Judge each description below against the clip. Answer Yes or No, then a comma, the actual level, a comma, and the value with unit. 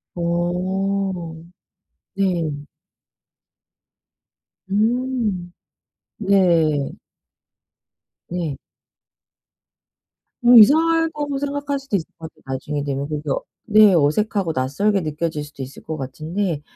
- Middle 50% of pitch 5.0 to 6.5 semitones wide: Yes, wide, 5.5 semitones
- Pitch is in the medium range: Yes, medium, 180 Hz